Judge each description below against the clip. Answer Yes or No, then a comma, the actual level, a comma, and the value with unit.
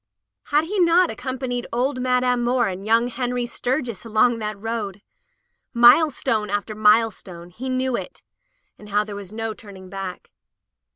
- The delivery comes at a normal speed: Yes, average, 155 wpm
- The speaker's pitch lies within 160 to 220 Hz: No, high, 230 Hz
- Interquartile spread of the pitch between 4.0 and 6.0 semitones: No, average, 3.3 semitones